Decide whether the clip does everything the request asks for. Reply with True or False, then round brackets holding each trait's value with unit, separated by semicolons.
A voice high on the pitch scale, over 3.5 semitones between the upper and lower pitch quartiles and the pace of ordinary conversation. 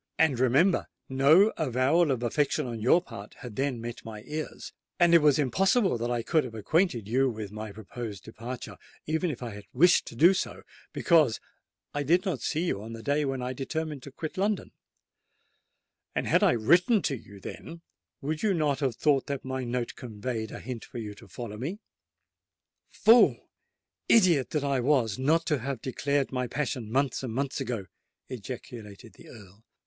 False (130 Hz; 5.0 semitones; 180 wpm)